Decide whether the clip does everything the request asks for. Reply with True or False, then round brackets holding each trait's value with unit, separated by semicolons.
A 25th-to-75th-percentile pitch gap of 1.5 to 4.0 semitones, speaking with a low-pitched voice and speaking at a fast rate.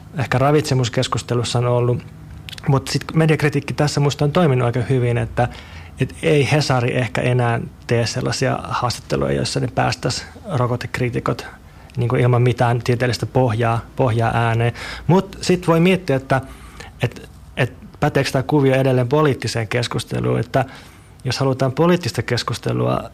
False (2.8 semitones; 125 Hz; 130 wpm)